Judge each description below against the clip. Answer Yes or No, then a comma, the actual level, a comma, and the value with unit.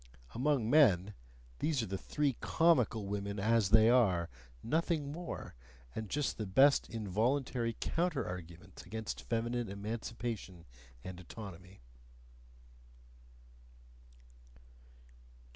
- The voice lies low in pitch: Yes, low, 115 Hz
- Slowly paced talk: Yes, slow, 95 wpm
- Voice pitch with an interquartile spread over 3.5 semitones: Yes, average, 5.3 semitones